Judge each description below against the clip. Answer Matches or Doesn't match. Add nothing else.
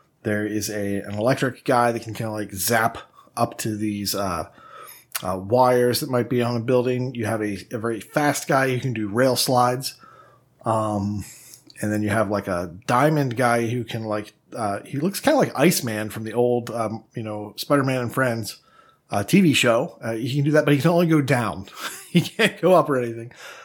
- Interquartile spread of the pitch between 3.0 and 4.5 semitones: Matches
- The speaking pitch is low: Matches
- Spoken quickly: Matches